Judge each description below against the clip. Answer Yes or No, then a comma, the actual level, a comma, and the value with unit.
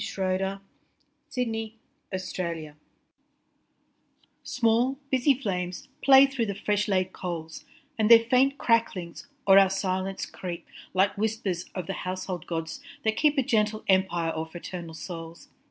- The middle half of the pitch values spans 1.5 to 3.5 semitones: No, average, 4.1 semitones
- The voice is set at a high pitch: Yes, high, 195 Hz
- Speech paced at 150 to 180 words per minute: No, average, 140 wpm